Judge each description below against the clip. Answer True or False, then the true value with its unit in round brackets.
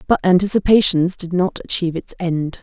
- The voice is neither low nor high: True (180 Hz)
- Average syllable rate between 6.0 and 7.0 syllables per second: False (5.6 syllables/s)